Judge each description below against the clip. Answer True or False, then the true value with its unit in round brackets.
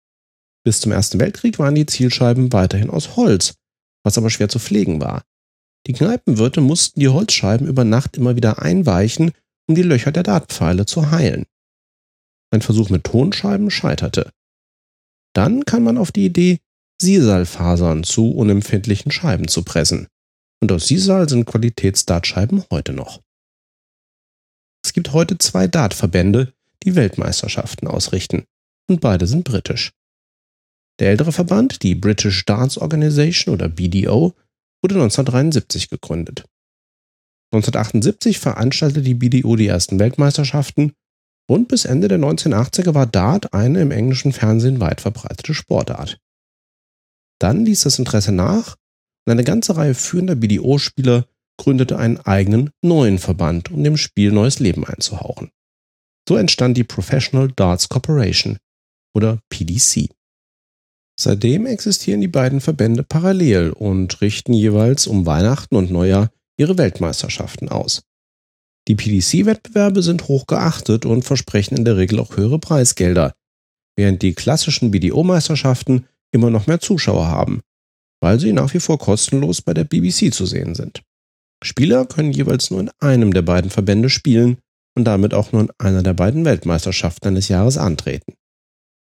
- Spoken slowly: False (135 wpm)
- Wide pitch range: True (7.3 semitones)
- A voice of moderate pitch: False (120 Hz)